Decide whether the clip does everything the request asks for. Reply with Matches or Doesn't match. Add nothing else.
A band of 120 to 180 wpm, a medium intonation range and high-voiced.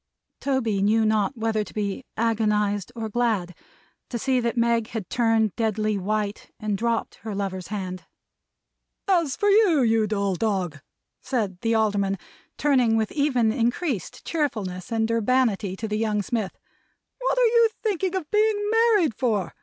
Matches